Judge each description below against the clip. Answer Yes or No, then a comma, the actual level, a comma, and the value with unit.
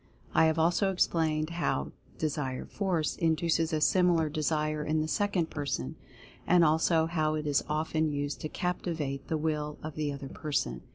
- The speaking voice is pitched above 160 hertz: No, medium, 155 Hz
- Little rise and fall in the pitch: Yes, narrow, 1.6 semitones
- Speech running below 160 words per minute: No, average, 165 wpm